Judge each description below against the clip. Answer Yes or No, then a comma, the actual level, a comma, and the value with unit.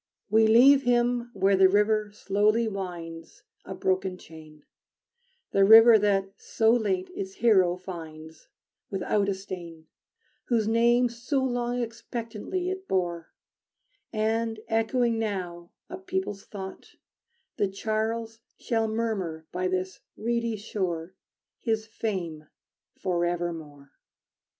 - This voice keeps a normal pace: No, slow, 110 wpm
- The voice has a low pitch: No, high, 210 Hz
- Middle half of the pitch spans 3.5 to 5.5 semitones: Yes, average, 3.9 semitones